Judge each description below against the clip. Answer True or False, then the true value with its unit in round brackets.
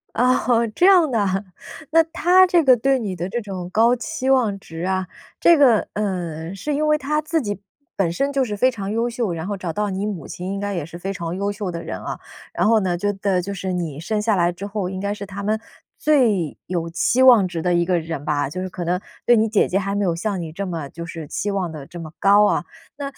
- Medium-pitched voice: False (200 Hz)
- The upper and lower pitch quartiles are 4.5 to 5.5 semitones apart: True (4.8 semitones)